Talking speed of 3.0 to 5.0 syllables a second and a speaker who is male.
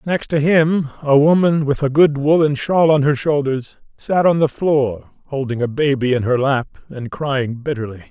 Yes: 4.6 syllables/s; male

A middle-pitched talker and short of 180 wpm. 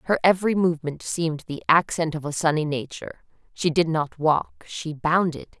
Yes: medium, 160 Hz; average, 160 wpm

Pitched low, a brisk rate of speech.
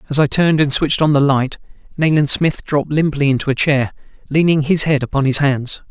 No: medium, 145 Hz; fast, 215 wpm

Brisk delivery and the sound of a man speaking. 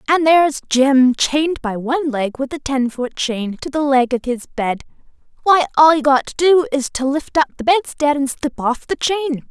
No: fast, 220 wpm; female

